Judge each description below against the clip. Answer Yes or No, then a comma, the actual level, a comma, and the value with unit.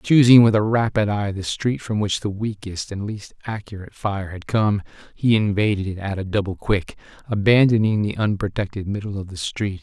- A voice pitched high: No, low, 105 Hz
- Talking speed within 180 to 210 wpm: Yes, average, 190 wpm